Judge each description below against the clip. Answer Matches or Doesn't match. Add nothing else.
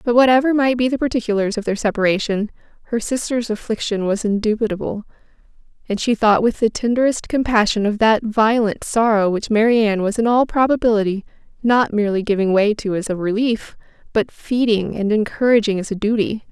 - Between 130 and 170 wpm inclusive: Matches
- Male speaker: Doesn't match